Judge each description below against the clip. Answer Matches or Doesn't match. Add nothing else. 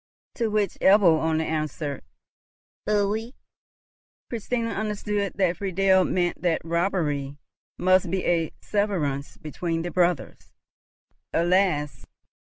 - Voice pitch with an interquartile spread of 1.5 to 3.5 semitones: Doesn't match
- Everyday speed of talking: Doesn't match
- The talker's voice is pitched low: Doesn't match